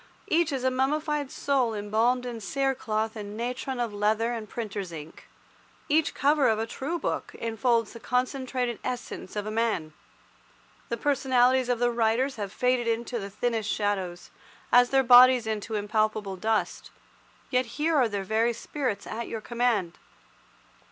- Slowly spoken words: No, average, 160 wpm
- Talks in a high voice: Yes, high, 235 Hz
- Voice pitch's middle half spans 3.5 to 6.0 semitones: No, average, 3.0 semitones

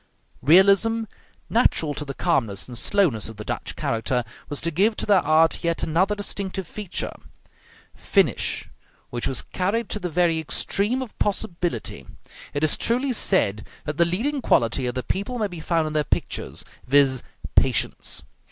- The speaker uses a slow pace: No, average, 160 wpm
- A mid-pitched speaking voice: Yes, medium, 170 Hz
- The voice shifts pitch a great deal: Yes, wide, 6.5 semitones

